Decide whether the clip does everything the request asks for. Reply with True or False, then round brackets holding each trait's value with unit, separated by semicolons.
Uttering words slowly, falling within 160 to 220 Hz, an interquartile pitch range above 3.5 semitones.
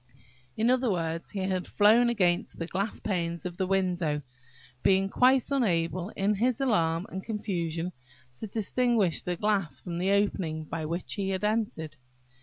False (160 wpm; 190 Hz; 3.9 semitones)